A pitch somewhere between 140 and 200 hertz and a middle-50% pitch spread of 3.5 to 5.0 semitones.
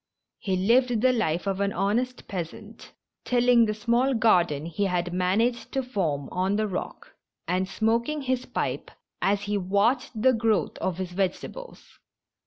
No: high, 210 Hz; average, 4.5 semitones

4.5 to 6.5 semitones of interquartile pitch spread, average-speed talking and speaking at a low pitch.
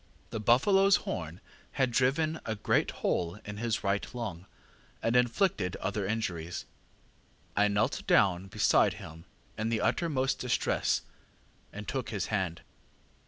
No: average, 4.8 semitones; slow, 130 wpm; low, 110 Hz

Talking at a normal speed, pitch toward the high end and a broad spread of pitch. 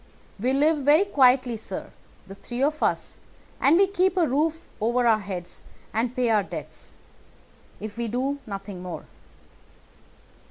Yes: average, 150 wpm; very high, 250 Hz; wide, 5.7 semitones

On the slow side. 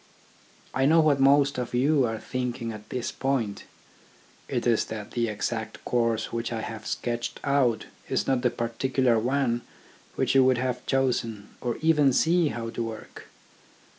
No: average, 165 wpm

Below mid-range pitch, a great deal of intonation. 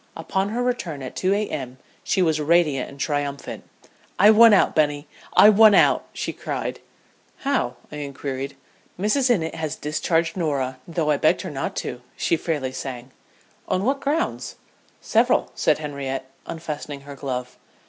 No: medium, 155 Hz; wide, 5.8 semitones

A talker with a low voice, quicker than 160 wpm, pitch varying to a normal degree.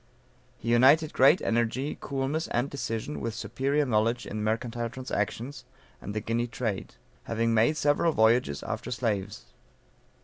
No: low, 120 Hz; slow, 135 wpm; average, 3.4 semitones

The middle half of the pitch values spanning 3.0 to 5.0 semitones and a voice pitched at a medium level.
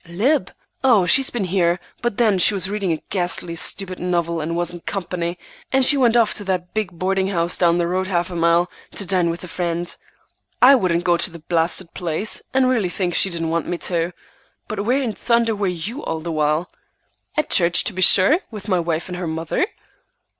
Yes: average, 3.5 semitones; medium, 180 Hz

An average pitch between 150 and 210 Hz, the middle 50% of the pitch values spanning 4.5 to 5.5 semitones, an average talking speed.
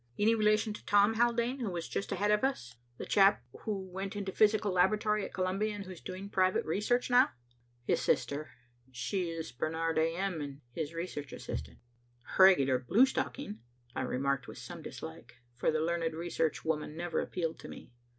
Yes: medium, 185 Hz; average, 4.8 semitones; average, 180 wpm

